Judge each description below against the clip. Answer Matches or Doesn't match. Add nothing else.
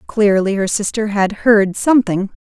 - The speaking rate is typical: Matches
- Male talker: Doesn't match